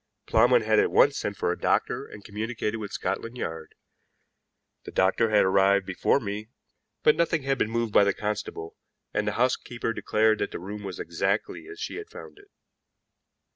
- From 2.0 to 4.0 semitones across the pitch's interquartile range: Yes, average, 3.1 semitones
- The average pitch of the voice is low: Yes, low, 105 Hz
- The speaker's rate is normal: Yes, average, 180 wpm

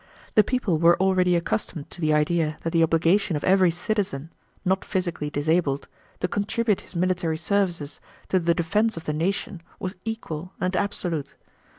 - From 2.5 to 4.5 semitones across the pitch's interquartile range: Yes, average, 3.0 semitones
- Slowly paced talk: No, average, 165 wpm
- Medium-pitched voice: Yes, medium, 175 Hz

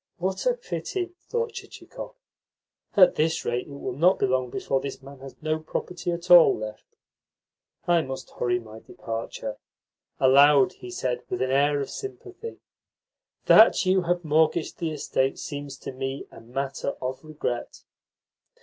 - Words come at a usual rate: Yes, average, 155 wpm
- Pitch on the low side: No, medium, 145 Hz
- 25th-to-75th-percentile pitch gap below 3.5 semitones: No, average, 5.1 semitones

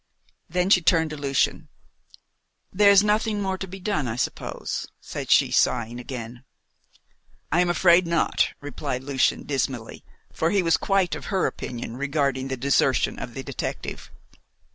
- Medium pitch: Yes, medium, 155 Hz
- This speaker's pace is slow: No, average, 155 wpm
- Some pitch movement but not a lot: No, wide, 6.1 semitones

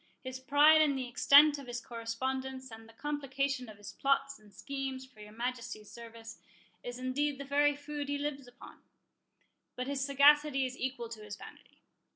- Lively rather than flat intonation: No, average, 2.9 semitones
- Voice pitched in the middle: No, very high, 265 Hz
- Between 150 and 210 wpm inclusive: Yes, average, 180 wpm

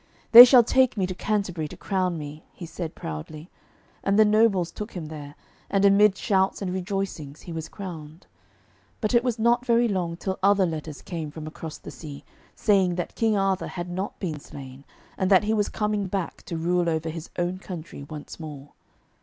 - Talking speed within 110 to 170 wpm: No, average, 195 wpm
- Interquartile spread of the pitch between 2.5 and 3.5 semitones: No, average, 4.2 semitones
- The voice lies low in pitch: No, medium, 180 Hz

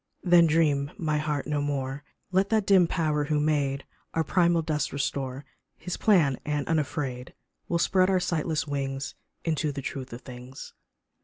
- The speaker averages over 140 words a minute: Yes, average, 160 wpm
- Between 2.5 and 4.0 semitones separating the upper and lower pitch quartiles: Yes, average, 3.2 semitones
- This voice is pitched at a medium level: Yes, medium, 150 Hz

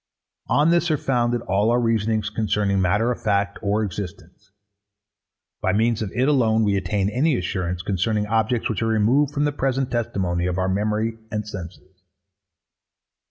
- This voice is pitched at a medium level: No, low, 110 Hz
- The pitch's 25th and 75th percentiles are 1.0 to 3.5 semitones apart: Yes, average, 3.2 semitones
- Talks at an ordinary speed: Yes, average, 160 wpm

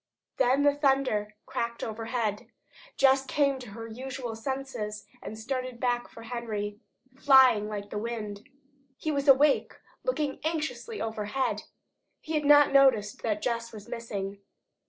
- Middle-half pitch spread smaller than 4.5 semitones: Yes, average, 4.0 semitones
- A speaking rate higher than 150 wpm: No, slow, 135 wpm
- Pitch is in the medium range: No, high, 240 Hz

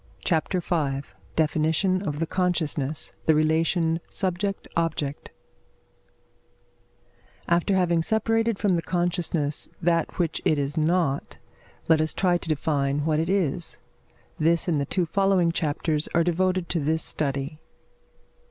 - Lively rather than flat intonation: No, average, 2.8 semitones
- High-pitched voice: No, medium, 165 Hz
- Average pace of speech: No, slow, 130 wpm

